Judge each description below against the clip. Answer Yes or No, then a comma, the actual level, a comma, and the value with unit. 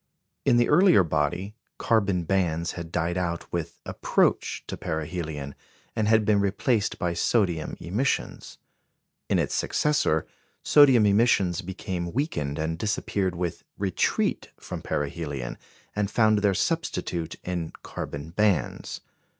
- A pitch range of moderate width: Yes, average, 4.4 semitones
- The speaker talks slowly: Yes, slow, 125 wpm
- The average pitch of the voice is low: Yes, very low, 90 Hz